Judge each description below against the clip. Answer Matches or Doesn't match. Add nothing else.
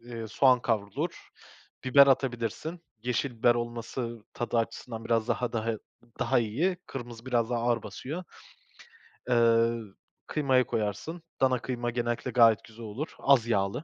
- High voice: Doesn't match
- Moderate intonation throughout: Doesn't match